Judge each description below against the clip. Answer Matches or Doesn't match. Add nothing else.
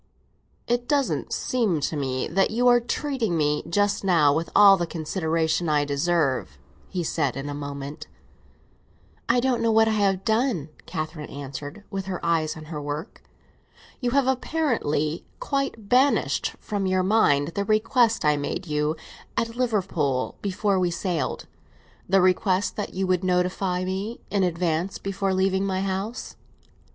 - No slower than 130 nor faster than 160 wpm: Matches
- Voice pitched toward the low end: Doesn't match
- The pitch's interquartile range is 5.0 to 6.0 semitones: Matches